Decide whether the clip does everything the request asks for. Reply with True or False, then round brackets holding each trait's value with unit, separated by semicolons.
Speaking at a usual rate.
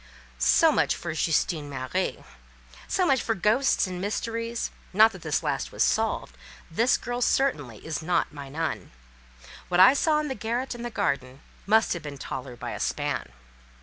True (165 wpm)